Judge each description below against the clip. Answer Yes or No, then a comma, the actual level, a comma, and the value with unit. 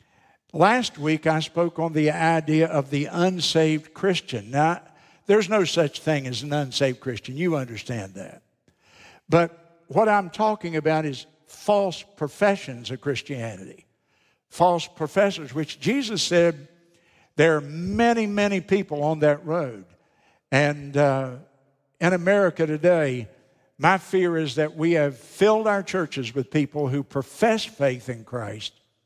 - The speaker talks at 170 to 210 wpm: No, average, 140 wpm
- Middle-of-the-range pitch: Yes, medium, 155 Hz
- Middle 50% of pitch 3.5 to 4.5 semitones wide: Yes, average, 4.2 semitones